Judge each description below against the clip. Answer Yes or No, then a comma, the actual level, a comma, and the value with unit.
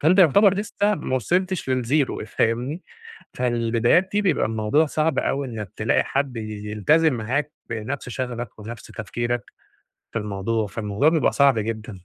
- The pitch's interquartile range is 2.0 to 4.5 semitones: No, wide, 5.6 semitones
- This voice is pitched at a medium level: No, low, 125 Hz